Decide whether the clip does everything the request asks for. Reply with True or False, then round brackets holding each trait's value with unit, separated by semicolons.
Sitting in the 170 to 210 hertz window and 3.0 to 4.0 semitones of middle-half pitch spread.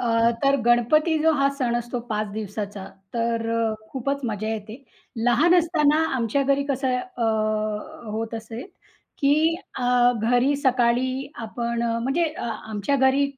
False (245 Hz; 3.3 semitones)